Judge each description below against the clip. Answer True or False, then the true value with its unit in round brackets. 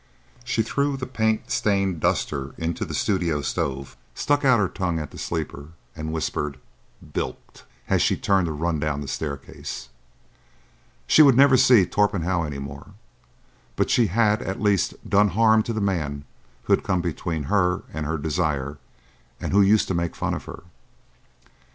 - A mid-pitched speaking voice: False (90 Hz)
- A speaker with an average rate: True (170 wpm)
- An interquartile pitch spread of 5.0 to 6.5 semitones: True (5.6 semitones)